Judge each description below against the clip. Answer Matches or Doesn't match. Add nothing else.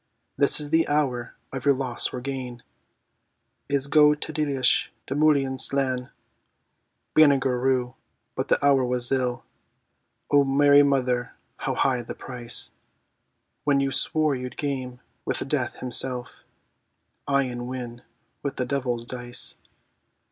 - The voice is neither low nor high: Doesn't match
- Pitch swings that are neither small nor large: Doesn't match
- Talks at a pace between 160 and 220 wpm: Doesn't match